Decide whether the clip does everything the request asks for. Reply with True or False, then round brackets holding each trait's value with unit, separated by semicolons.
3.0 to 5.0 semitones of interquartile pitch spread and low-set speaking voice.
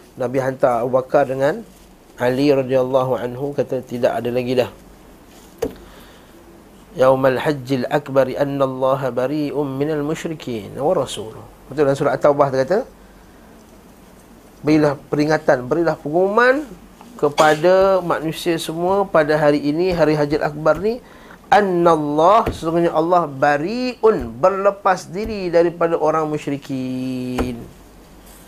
False (4.4 semitones; 150 Hz)